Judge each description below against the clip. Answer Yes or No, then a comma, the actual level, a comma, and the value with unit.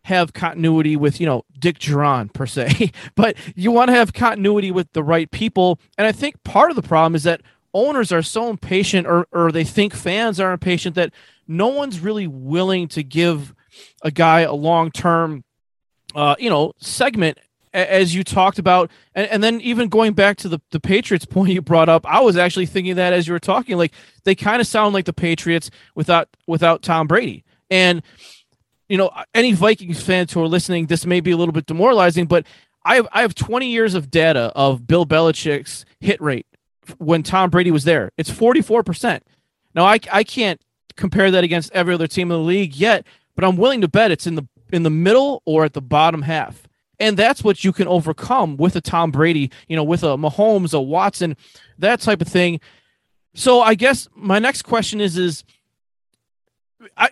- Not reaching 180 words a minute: No, average, 200 wpm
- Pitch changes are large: No, average, 3.7 semitones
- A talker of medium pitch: Yes, medium, 175 Hz